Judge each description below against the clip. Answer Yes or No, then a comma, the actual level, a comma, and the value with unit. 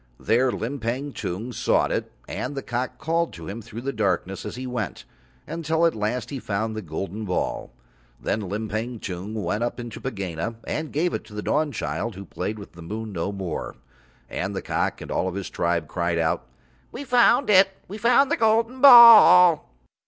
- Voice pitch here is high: No, low, 115 Hz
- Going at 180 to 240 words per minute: Yes, average, 185 wpm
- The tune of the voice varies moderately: No, wide, 8.0 semitones